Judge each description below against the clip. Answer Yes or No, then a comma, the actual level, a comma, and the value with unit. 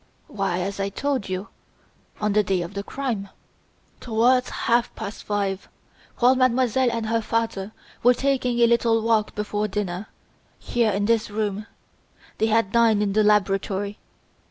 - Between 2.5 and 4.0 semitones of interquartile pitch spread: Yes, average, 2.8 semitones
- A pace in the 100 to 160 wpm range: Yes, average, 155 wpm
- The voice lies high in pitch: Yes, high, 215 Hz